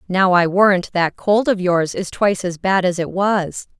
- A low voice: No, medium, 185 Hz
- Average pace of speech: No, fast, 220 wpm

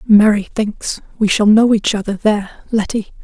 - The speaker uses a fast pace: No, average, 165 wpm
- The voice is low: No, high, 210 Hz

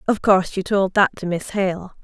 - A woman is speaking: Yes, female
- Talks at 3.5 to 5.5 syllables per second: Yes, 5.1 syllables/s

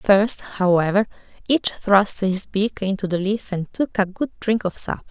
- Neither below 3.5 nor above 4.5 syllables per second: Yes, 4.2 syllables/s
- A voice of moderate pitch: No, high, 200 Hz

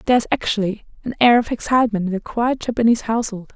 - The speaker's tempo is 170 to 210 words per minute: Yes, fast, 205 wpm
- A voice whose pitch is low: No, high, 225 Hz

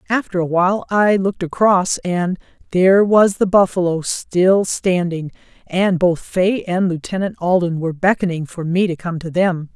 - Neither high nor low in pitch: Yes, medium, 180 Hz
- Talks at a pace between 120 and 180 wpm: Yes, average, 165 wpm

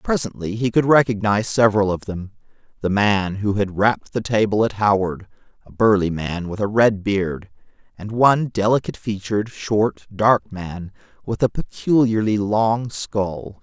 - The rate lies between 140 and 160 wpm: Yes, average, 155 wpm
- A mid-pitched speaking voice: No, low, 105 Hz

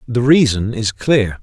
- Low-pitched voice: Yes, low, 115 Hz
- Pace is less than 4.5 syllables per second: Yes, 3.9 syllables/s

